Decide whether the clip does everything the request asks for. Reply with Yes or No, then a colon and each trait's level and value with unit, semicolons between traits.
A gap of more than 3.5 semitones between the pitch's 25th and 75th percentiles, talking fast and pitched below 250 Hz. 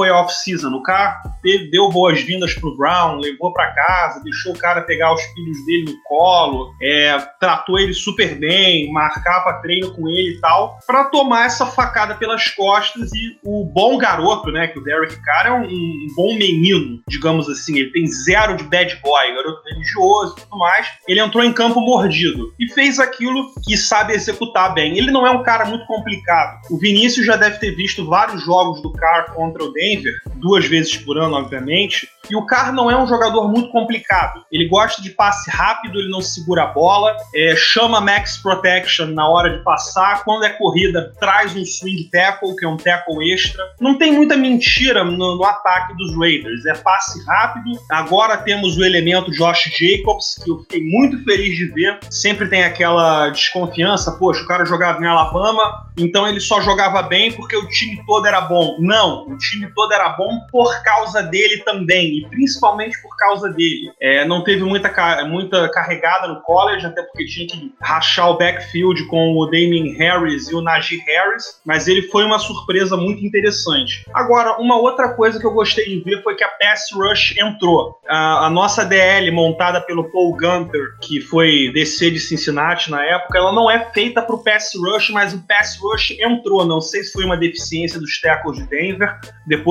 Yes: average, 4.3 semitones; fast, 190 wpm; medium, 185 Hz